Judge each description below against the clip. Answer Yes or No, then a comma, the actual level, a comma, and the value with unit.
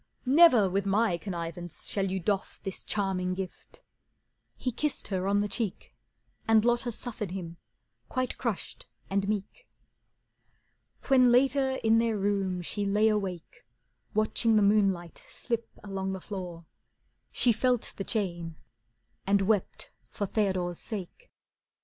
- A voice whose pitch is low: No, high, 200 Hz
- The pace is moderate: No, slow, 130 wpm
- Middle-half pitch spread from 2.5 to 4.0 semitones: Yes, average, 3.2 semitones